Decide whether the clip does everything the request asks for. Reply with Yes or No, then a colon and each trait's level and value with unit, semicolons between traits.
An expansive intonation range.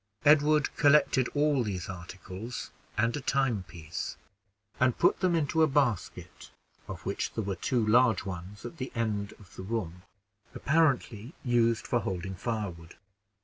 Yes: wide, 6.2 semitones